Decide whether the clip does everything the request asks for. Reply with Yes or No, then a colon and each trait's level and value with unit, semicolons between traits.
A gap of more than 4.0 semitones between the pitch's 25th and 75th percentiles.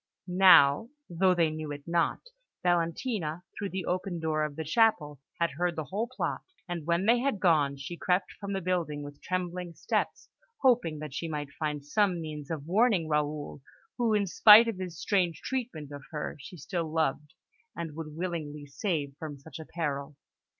No: average, 3.6 semitones